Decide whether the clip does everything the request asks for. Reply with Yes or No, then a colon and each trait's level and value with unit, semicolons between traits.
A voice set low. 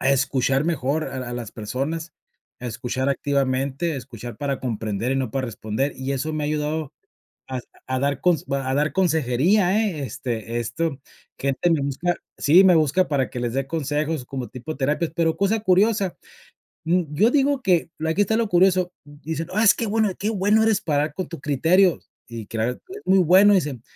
No: medium, 150 Hz